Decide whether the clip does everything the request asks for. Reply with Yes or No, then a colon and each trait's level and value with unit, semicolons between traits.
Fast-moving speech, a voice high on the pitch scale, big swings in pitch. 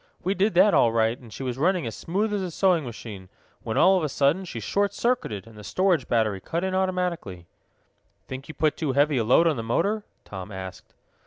No: fast, 225 wpm; medium, 150 Hz; wide, 8.6 semitones